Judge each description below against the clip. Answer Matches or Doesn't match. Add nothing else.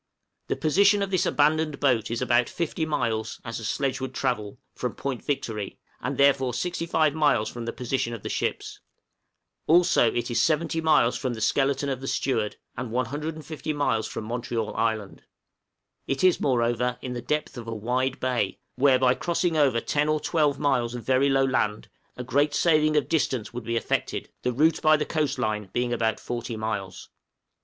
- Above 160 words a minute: Matches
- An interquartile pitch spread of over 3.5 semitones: Matches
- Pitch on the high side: Doesn't match